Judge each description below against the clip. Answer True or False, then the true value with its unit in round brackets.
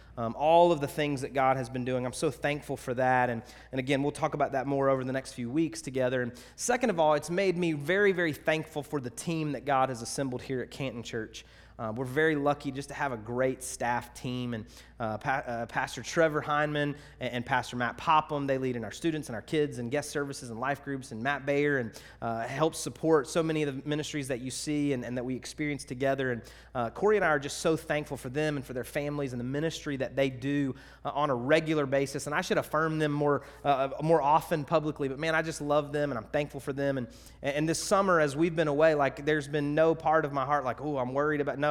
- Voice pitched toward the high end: False (140 Hz)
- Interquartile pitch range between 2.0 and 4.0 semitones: True (3.0 semitones)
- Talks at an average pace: False (255 wpm)